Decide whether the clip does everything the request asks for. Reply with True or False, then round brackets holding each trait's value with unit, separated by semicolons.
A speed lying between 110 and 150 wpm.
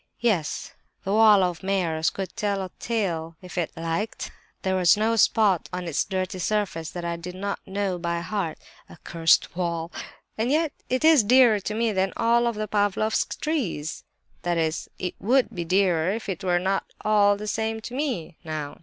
False (175 wpm)